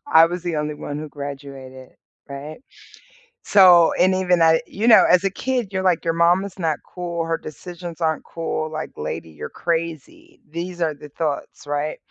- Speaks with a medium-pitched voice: Yes, medium, 165 Hz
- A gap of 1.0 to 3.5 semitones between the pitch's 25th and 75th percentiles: Yes, average, 3.0 semitones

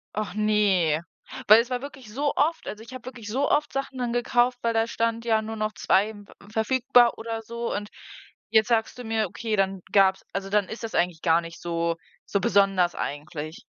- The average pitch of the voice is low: No, high, 220 Hz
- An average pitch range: Yes, average, 3.4 semitones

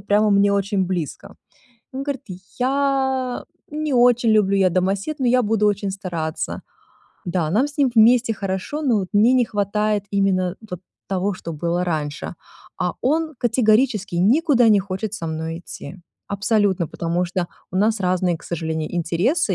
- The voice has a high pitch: Yes, high, 200 Hz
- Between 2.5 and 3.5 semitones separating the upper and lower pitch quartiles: No, average, 5.0 semitones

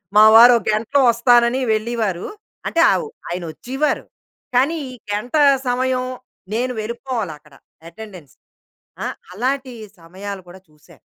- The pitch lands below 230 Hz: No, high, 235 Hz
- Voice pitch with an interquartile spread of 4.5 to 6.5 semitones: Yes, average, 4.9 semitones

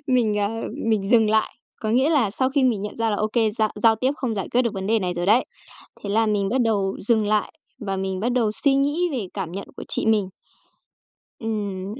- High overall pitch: Yes, high, 220 Hz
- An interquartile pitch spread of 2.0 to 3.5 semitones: Yes, average, 3.2 semitones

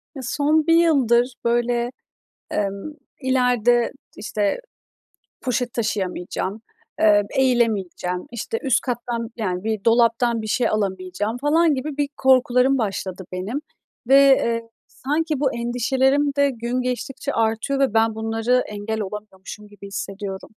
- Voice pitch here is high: Yes, high, 235 Hz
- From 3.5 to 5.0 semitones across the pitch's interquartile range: Yes, average, 3.8 semitones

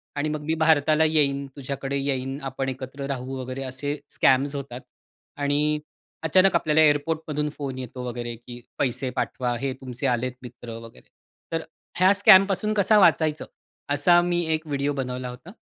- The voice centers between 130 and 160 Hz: Yes, medium, 140 Hz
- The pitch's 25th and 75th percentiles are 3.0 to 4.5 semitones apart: Yes, average, 3.3 semitones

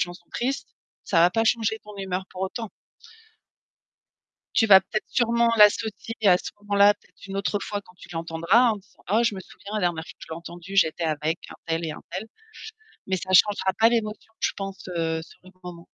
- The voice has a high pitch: Yes, high, 195 Hz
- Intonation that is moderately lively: Yes, average, 3.6 semitones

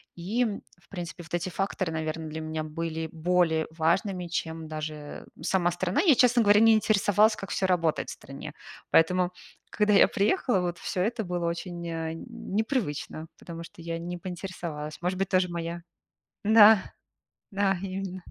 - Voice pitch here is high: No, medium, 175 Hz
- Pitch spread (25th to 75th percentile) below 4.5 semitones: Yes, average, 3.1 semitones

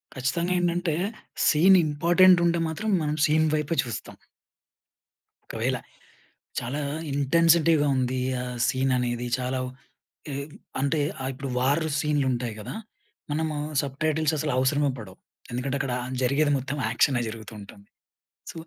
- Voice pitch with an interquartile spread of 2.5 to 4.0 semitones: Yes, average, 3.6 semitones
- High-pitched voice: No, medium, 145 Hz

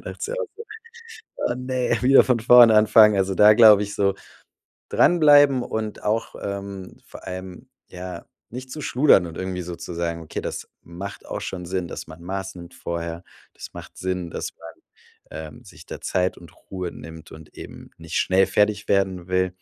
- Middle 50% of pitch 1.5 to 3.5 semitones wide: No, average, 4.0 semitones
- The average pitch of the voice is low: Yes, very low, 95 Hz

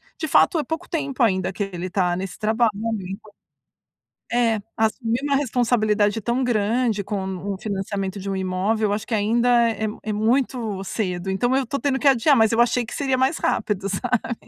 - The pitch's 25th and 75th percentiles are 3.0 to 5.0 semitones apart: Yes, average, 3.9 semitones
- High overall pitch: Yes, high, 220 Hz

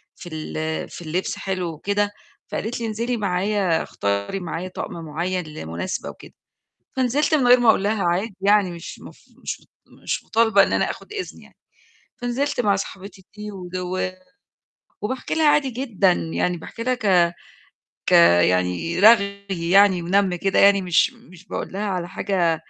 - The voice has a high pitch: Yes, high, 195 Hz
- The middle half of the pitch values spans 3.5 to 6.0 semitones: Yes, average, 4.2 semitones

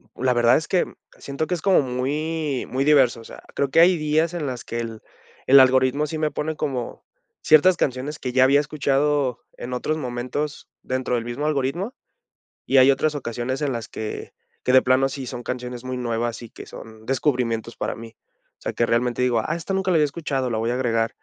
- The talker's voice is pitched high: No, low, 130 Hz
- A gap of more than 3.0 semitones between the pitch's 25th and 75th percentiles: Yes, average, 3.6 semitones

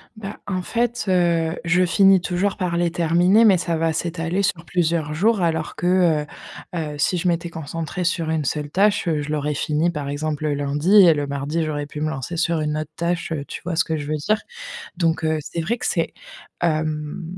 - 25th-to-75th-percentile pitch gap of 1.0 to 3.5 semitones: Yes, average, 2.8 semitones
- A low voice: No, medium, 165 Hz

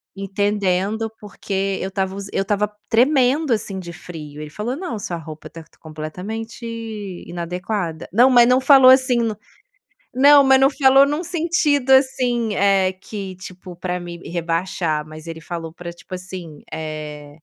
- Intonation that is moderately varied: No, wide, 6.3 semitones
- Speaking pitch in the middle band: No, high, 195 Hz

